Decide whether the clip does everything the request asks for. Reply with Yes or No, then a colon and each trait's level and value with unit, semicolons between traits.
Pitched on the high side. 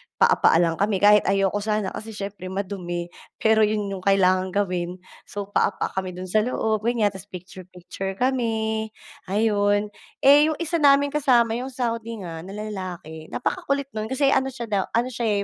Yes: high, 205 Hz